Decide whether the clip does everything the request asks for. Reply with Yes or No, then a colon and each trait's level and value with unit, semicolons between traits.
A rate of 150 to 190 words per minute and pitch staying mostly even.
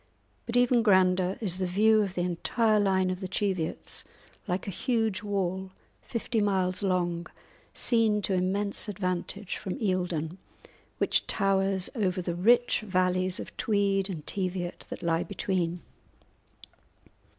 No: slow, 135 wpm; narrow, 2.3 semitones